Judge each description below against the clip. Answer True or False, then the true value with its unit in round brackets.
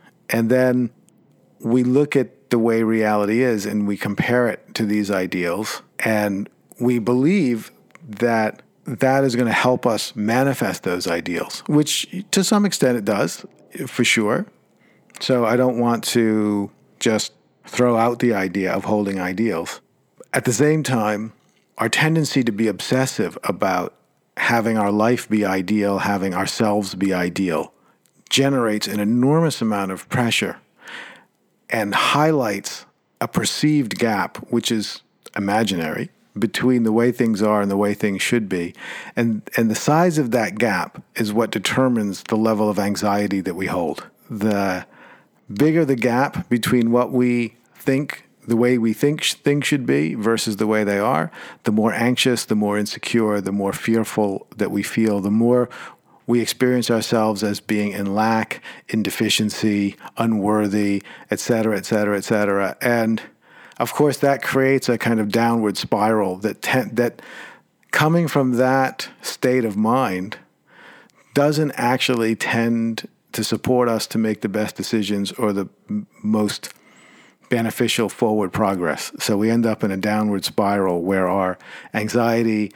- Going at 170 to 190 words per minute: False (150 wpm)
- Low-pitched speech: True (115 Hz)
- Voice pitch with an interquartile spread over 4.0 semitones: False (3.3 semitones)